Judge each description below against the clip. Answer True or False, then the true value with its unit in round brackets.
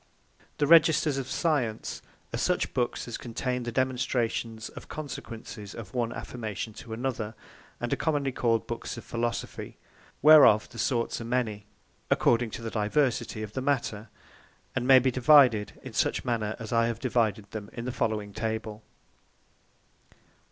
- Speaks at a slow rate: False (155 wpm)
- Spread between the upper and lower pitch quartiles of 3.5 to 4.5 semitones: False (2.8 semitones)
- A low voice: True (120 Hz)